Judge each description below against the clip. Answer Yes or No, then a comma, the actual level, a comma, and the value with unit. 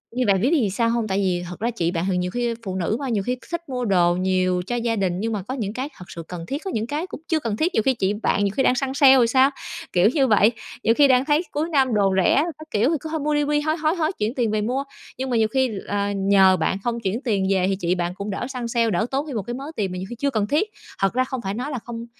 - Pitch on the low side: No, high, 230 Hz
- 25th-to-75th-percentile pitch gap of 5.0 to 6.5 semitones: Yes, wide, 5.4 semitones